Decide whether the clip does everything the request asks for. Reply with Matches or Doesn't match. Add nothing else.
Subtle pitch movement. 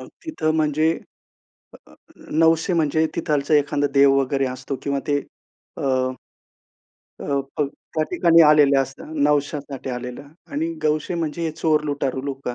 Matches